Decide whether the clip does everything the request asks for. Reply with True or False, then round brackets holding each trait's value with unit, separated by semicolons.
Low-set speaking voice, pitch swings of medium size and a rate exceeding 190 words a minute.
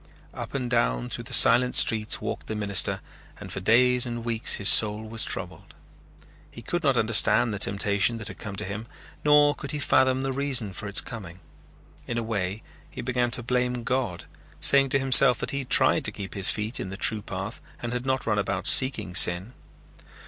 True (115 Hz; 3.8 semitones; 205 wpm)